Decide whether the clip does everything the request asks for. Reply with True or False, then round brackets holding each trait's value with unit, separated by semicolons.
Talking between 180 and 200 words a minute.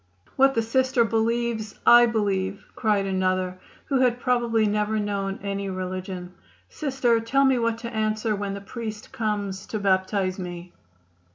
False (150 wpm)